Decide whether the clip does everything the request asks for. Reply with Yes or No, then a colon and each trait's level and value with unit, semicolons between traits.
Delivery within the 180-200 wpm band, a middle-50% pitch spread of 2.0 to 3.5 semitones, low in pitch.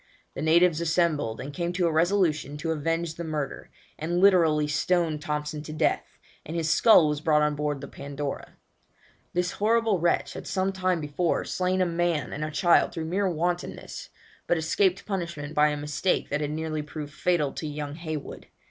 No: average, 185 wpm; average, 2.8 semitones; medium, 160 Hz